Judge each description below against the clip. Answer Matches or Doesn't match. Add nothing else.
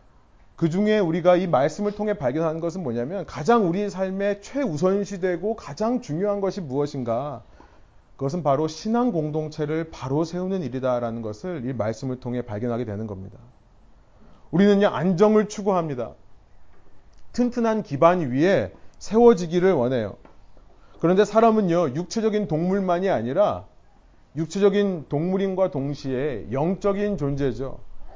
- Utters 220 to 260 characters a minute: Doesn't match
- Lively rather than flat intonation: Matches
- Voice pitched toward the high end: Doesn't match